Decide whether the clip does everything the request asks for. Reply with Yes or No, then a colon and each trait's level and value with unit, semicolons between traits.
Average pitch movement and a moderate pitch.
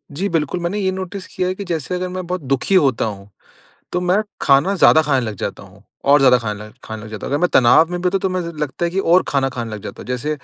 No: wide, 6.0 semitones; medium, 160 Hz